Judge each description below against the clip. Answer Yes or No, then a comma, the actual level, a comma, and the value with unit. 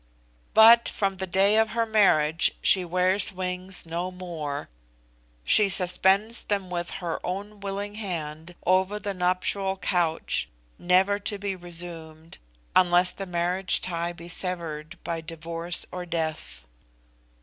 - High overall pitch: No, medium, 180 Hz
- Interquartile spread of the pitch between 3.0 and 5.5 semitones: No, narrow, 2.5 semitones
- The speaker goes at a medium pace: No, slow, 130 wpm